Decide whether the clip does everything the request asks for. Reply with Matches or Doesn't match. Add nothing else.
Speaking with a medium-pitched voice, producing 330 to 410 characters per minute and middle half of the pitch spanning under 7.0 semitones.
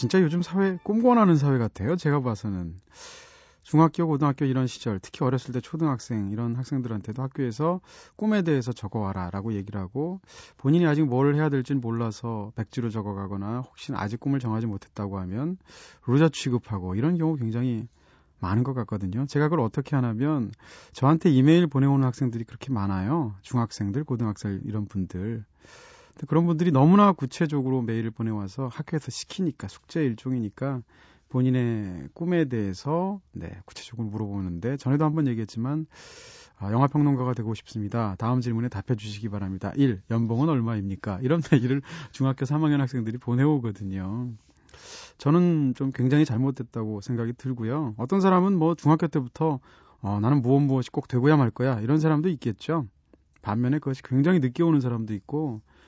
Doesn't match